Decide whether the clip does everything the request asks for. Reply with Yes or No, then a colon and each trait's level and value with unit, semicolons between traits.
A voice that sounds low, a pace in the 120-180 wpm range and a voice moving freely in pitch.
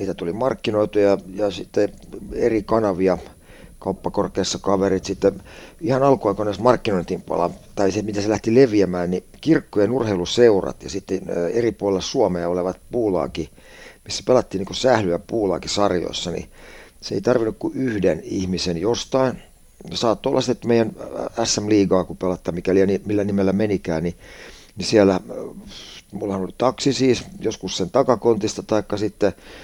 No: low, 100 Hz; average, 135 wpm; average, 3.3 semitones